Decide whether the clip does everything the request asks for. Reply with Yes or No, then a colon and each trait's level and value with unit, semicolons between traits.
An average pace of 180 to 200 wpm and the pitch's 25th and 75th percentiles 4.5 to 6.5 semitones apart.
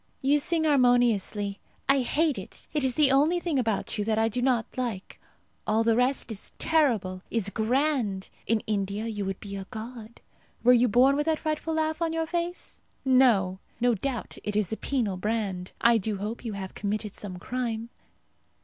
Yes: average, 185 wpm; average, 4.8 semitones